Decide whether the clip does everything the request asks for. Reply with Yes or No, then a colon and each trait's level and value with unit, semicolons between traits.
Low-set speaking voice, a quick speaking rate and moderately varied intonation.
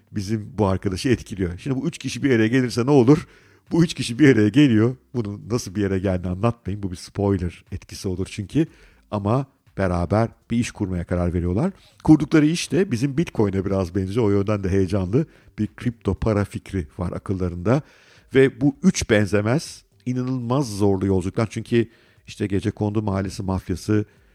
Yes: low, 105 Hz; fast, 165 wpm; average, 4.4 semitones